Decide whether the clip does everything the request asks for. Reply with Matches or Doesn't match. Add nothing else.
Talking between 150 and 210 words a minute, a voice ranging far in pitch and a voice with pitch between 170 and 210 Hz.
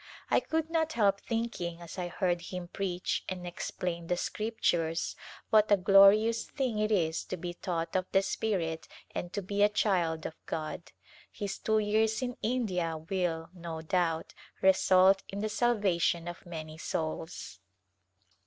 Doesn't match